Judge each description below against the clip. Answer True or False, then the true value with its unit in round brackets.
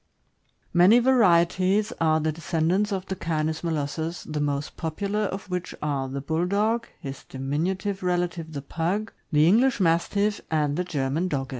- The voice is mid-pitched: True (170 Hz)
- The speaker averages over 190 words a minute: False (155 wpm)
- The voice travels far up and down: False (4.1 semitones)